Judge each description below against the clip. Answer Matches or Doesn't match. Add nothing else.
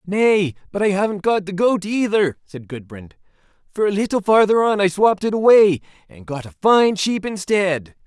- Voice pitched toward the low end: Doesn't match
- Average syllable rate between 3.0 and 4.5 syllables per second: Doesn't match